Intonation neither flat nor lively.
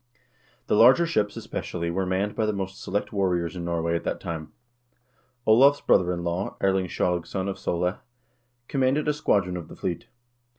Yes: average, 3.3 semitones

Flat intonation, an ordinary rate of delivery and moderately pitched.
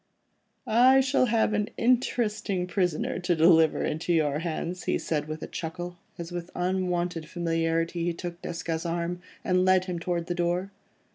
Yes: narrow, 1.9 semitones; average, 160 wpm; medium, 175 Hz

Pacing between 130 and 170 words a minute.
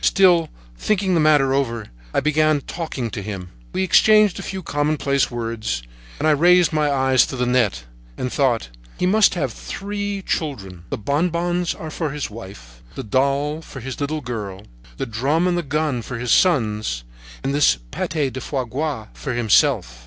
No: average, 180 wpm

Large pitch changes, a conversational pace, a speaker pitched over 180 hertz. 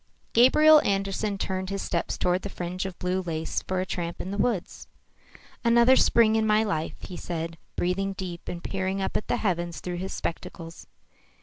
No: average, 2.7 semitones; average, 185 wpm; high, 190 Hz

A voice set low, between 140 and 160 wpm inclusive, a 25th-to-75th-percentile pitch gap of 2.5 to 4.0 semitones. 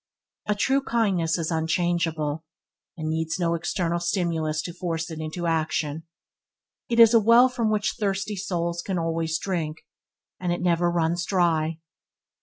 No: medium, 170 Hz; average, 150 wpm; average, 2.9 semitones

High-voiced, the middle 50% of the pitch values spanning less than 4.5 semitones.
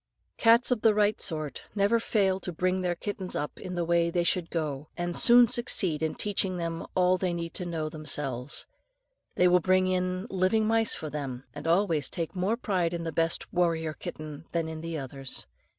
No: medium, 175 Hz; average, 3.0 semitones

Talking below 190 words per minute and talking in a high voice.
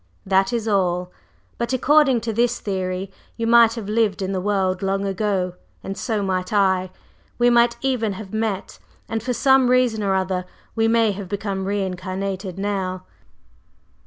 Yes: average, 165 wpm; high, 200 Hz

